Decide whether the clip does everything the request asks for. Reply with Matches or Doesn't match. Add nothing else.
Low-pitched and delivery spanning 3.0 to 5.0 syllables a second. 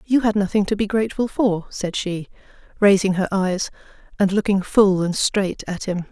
Doesn't match